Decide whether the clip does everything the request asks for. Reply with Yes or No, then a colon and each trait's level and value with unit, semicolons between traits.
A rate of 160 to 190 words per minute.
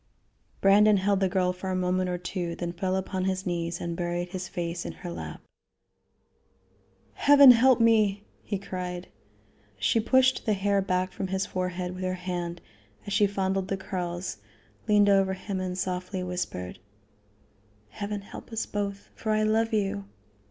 Yes: average, 165 wpm